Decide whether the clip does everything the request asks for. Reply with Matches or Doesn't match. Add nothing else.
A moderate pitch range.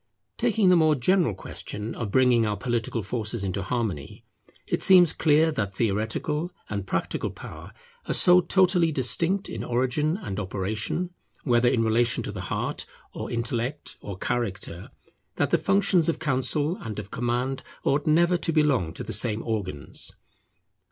Doesn't match